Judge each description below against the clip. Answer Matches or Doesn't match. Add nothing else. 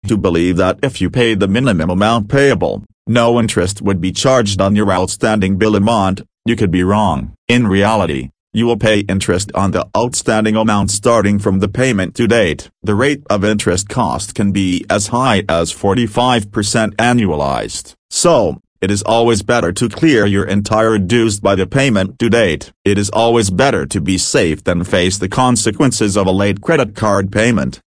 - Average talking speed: Matches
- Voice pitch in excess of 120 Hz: Doesn't match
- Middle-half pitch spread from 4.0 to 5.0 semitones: Doesn't match